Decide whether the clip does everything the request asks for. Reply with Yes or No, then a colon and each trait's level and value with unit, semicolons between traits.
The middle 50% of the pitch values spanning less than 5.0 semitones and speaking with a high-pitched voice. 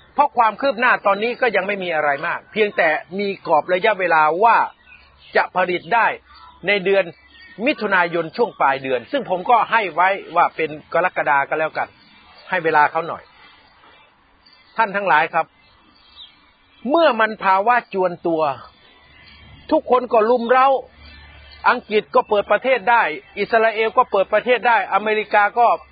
No: wide, 5.4 semitones; high, 205 Hz